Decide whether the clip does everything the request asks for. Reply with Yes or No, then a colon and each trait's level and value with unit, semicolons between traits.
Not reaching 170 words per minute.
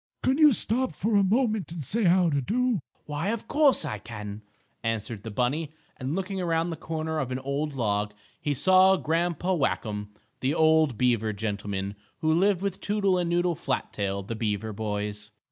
No: average, 180 wpm